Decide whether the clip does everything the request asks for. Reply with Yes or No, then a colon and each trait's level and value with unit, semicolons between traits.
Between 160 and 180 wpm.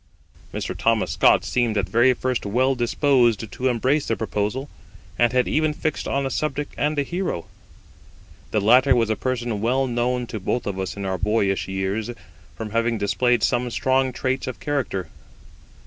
Yes: average, 175 wpm